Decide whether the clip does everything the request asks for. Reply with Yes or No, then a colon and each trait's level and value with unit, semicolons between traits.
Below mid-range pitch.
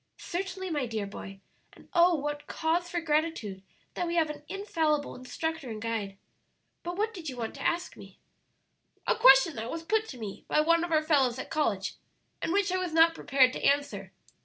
No: very high, 310 Hz